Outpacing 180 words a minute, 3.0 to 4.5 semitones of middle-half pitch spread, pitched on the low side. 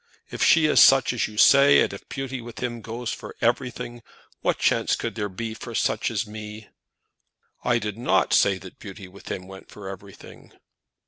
Yes: average, 190 wpm; average, 3.3 semitones; low, 110 Hz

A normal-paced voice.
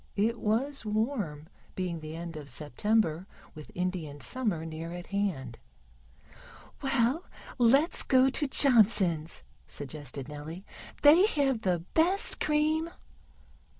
No: slow, 115 wpm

